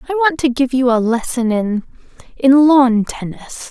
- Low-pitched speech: No, very high, 255 Hz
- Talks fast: No, average, 160 wpm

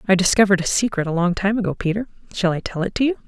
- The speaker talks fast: Yes, fast, 275 wpm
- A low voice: No, high, 190 Hz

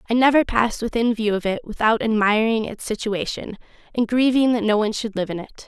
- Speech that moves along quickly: Yes, fast, 210 wpm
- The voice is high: Yes, high, 220 Hz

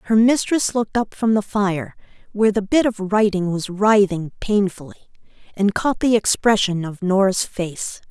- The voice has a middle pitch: No, high, 205 Hz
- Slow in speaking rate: No, average, 165 wpm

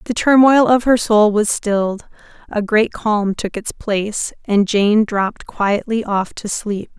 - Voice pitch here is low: No, high, 215 Hz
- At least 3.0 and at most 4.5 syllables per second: Yes, 4.0 syllables/s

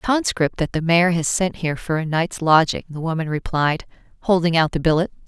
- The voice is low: No, medium, 165 Hz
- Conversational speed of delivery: No, fast, 215 wpm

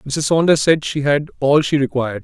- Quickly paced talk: Yes, fast, 215 wpm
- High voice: No, medium, 145 Hz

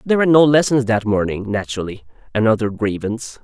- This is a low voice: Yes, low, 115 Hz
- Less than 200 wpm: Yes, average, 140 wpm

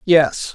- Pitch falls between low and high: Yes, medium, 160 Hz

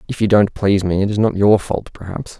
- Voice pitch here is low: Yes, low, 100 Hz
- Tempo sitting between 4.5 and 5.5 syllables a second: No, 6.0 syllables/s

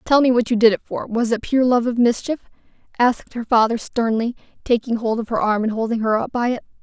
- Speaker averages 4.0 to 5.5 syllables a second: No, 6.0 syllables/s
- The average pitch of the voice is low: No, high, 235 Hz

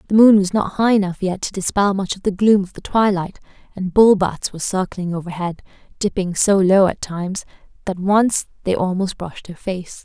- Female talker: Yes, female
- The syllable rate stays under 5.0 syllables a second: No, 5.3 syllables/s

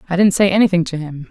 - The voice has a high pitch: No, medium, 180 Hz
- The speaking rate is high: Yes, fast, 275 wpm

